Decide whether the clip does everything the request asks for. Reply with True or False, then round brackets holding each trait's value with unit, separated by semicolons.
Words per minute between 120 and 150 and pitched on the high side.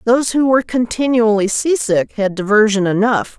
True (140 wpm; 225 Hz)